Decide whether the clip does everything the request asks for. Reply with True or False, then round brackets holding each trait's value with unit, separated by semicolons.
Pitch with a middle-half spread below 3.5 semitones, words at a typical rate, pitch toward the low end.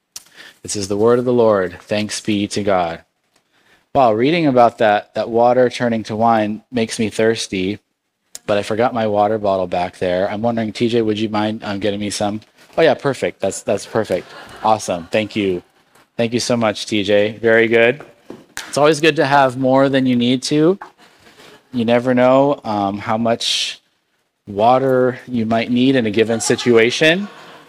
True (2.8 semitones; 180 wpm; 115 Hz)